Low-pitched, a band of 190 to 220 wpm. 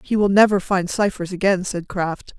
No: high, 190 Hz; average, 200 wpm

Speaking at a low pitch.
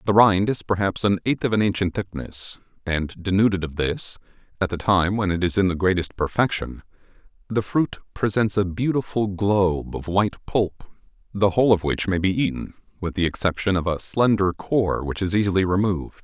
Yes: very low, 95 Hz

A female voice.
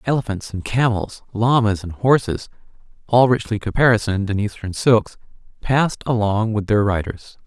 No: male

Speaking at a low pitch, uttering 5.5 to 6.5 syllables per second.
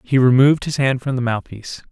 Yes: low, 125 Hz; 6.3 syllables/s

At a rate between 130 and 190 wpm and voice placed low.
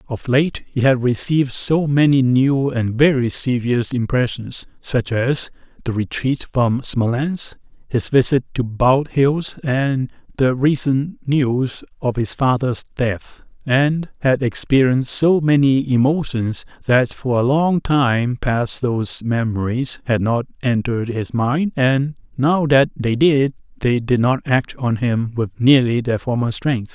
Yes: average, 140 wpm; low, 130 Hz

